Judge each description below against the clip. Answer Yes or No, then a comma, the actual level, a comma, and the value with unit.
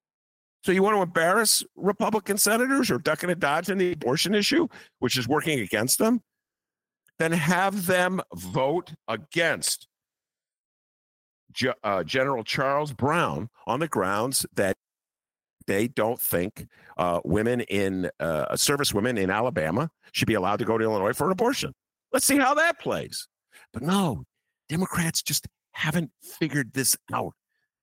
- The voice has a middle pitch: Yes, medium, 155 Hz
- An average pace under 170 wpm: Yes, average, 150 wpm